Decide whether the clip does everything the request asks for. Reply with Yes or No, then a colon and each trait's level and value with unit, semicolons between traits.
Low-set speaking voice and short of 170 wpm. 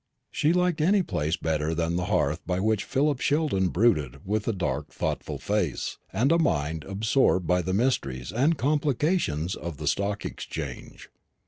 Yes: low, 100 Hz; average, 160 wpm